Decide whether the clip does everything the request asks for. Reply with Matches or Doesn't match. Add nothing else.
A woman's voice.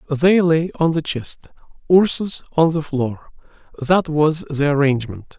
Doesn't match